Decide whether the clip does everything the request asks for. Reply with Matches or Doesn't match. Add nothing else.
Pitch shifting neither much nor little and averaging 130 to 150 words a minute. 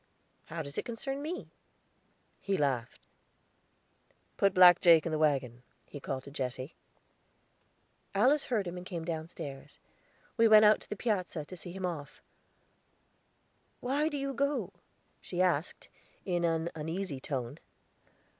Doesn't match